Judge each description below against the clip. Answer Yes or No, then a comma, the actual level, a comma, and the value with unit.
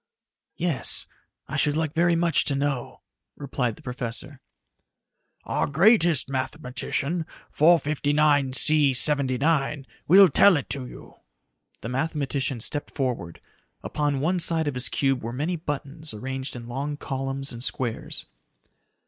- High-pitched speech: No, medium, 140 Hz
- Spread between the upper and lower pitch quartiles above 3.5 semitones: No, average, 3.0 semitones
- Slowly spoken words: Yes, slow, 125 wpm